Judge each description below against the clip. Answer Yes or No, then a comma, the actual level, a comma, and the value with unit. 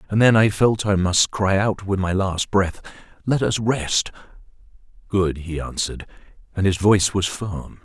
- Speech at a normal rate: Yes, average, 175 wpm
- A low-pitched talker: Yes, low, 100 Hz